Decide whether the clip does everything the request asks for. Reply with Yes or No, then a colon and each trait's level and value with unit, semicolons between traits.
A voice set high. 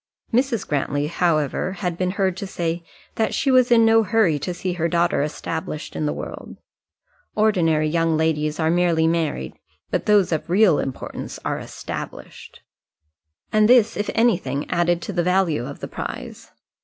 No: medium, 175 Hz